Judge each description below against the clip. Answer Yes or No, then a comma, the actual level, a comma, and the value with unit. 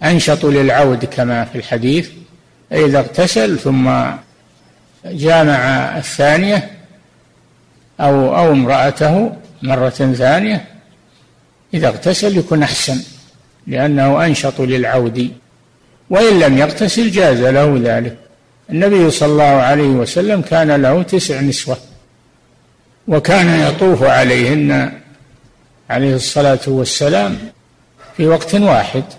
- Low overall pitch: No, medium, 145 Hz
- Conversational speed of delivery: Yes, average, 95 wpm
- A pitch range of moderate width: Yes, average, 4.3 semitones